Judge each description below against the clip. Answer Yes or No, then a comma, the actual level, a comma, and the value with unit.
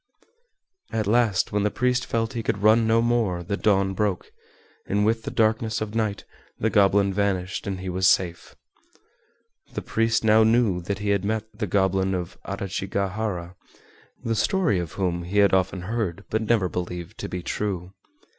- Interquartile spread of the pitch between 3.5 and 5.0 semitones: No, average, 2.9 semitones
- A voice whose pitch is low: Yes, low, 100 Hz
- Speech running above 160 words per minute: Yes, average, 175 wpm